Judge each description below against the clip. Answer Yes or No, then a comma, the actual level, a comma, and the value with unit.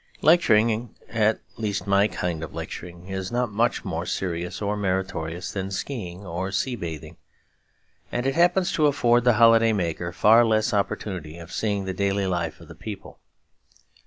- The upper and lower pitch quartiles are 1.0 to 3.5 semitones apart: No, average, 4.3 semitones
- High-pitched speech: No, low, 100 Hz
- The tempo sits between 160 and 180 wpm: Yes, average, 165 wpm